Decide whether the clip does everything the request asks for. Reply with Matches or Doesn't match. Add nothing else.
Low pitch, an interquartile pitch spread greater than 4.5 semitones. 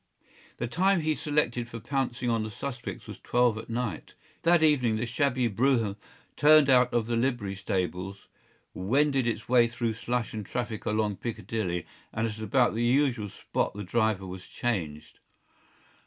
Doesn't match